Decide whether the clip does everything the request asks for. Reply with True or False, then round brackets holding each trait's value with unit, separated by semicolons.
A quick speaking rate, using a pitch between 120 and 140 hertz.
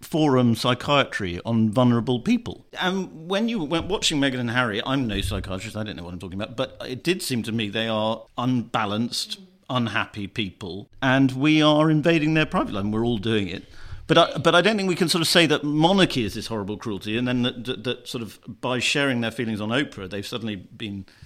True (225 wpm; 125 Hz)